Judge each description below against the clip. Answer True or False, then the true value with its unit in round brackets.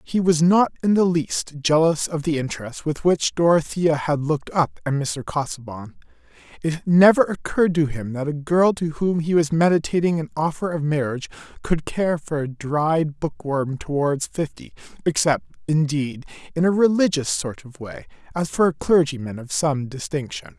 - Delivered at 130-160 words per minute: False (170 wpm)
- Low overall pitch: False (155 Hz)